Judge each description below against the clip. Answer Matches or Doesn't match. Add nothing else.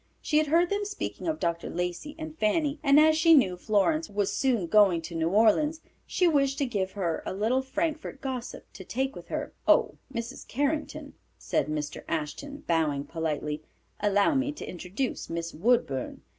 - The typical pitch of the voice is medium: Doesn't match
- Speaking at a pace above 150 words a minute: Matches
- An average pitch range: Doesn't match